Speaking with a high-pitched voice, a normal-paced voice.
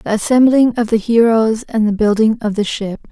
No: high, 225 Hz; fast, 210 wpm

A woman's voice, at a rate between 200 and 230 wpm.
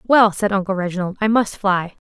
Yes: female; fast, 205 wpm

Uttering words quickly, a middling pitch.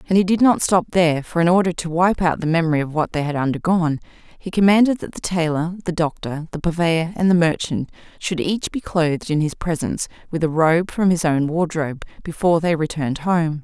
Yes: fast, 215 wpm; medium, 170 Hz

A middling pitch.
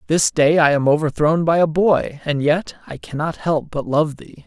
Yes: medium, 155 Hz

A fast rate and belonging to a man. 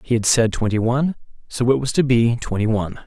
Yes: fast, 235 wpm; male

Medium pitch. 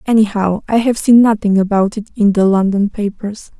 No: high, 210 Hz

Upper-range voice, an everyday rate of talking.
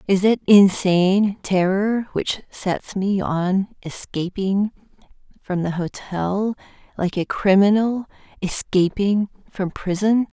No: high, 195 Hz; slow, 105 wpm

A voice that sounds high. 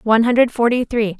Yes: high, 230 Hz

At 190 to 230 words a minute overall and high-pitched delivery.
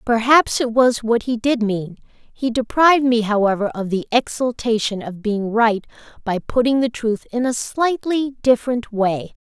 No: average, 165 wpm; high, 230 Hz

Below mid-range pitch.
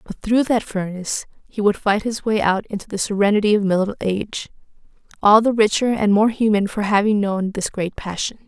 No: high, 210 Hz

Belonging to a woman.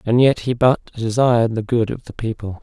No: male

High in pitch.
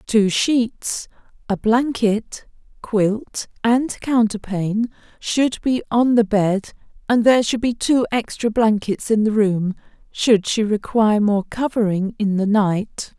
Yes: high, 220 Hz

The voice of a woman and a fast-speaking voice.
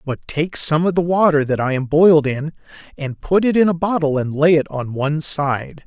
No: male; fast, 235 wpm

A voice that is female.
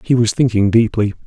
No: male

